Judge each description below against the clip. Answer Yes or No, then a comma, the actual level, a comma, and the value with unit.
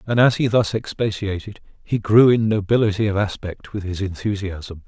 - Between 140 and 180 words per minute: Yes, average, 170 wpm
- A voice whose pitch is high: No, low, 105 Hz